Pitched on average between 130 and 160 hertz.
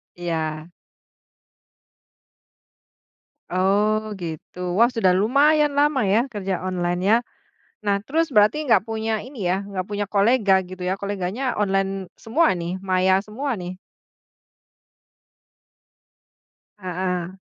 No: high, 200 Hz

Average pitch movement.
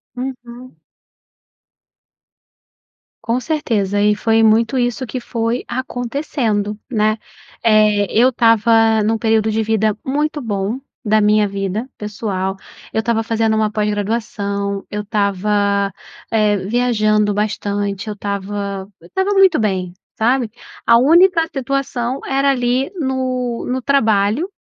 Yes: average, 3.2 semitones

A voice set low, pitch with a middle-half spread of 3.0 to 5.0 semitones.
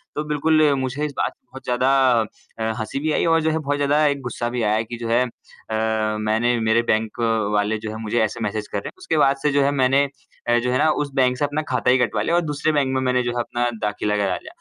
Yes: low, 125 Hz; average, 4.3 semitones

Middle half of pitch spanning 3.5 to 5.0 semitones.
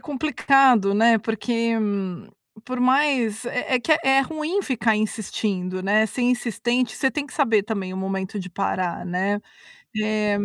Yes: average, 4.2 semitones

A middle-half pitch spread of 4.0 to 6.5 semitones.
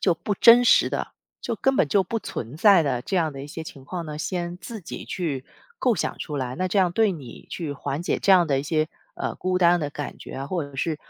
Yes: average, 4.5 semitones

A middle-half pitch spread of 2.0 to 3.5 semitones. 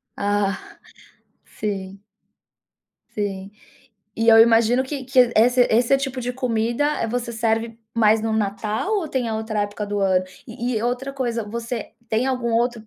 Yes: narrow, 2.5 semitones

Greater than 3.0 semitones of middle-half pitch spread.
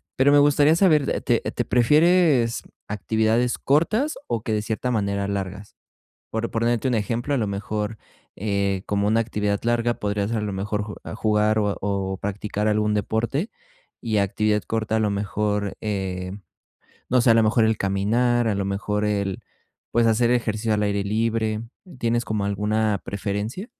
No: narrow, 2.4 semitones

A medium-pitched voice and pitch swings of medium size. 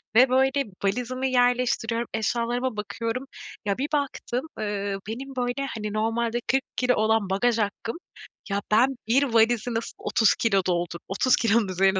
No: high, 230 Hz; average, 3.0 semitones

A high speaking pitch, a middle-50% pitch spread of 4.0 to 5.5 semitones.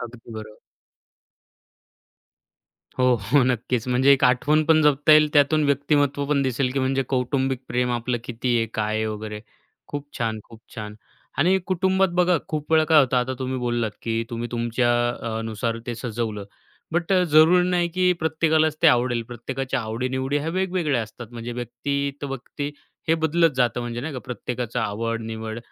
No: low, 130 Hz; average, 4.3 semitones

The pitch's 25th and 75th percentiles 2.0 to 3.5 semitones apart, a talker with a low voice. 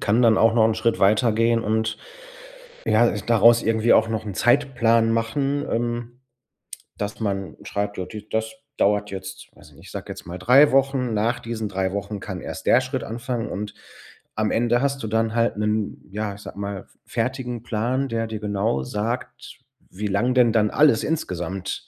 Yes: narrow, 2.6 semitones; low, 110 Hz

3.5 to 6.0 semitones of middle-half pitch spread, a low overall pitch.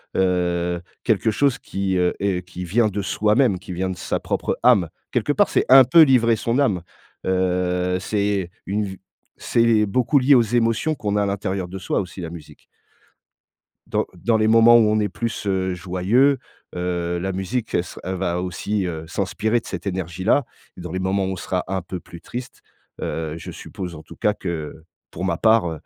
Yes: average, 3.8 semitones; very low, 95 Hz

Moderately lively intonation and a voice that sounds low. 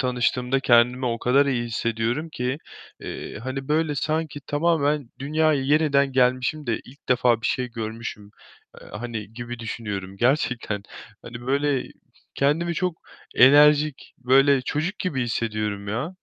Yes: average, 3.7 semitones; low, 130 Hz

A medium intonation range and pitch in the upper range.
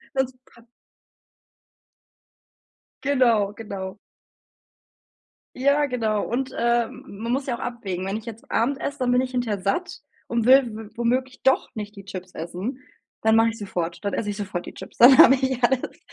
Yes: average, 4.0 semitones; high, 235 Hz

